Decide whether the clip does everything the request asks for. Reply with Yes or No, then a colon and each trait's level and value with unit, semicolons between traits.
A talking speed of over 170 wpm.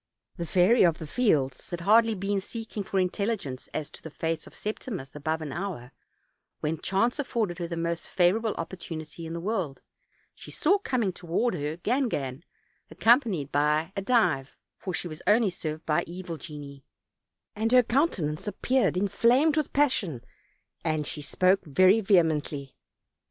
No: average, 160 wpm